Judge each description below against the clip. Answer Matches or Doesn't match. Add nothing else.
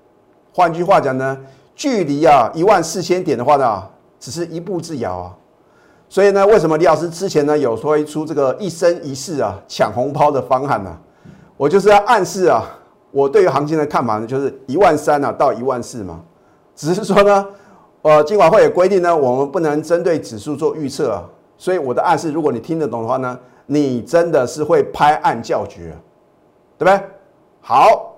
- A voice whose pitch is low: Doesn't match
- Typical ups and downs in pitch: Doesn't match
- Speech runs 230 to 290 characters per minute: Matches